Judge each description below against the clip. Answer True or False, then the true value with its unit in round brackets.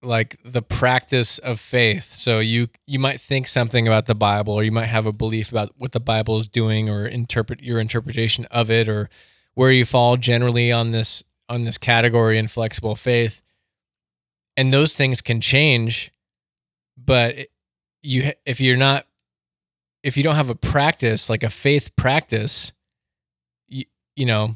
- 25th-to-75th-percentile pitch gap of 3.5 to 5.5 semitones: False (2.7 semitones)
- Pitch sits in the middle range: False (115 Hz)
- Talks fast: False (165 wpm)